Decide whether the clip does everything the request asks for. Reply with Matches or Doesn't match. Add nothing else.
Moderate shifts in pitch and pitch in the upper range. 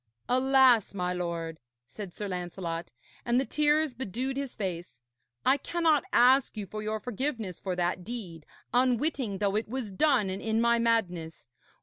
Doesn't match